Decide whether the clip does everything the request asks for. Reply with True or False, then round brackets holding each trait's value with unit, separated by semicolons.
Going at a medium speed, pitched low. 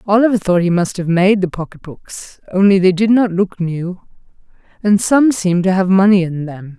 False (195 wpm; 190 Hz)